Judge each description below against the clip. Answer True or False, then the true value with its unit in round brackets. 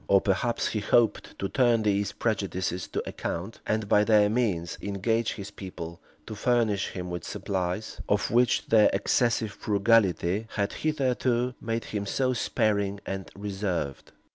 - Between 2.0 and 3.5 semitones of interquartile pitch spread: True (2.9 semitones)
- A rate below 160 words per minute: True (145 wpm)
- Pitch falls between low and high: False (105 Hz)